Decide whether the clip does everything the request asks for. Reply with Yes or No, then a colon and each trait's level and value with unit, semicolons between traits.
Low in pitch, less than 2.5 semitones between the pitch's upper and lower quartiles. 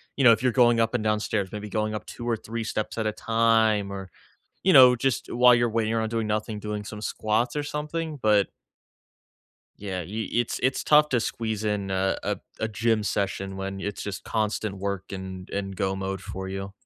No: low, 110 Hz; average, 2.9 semitones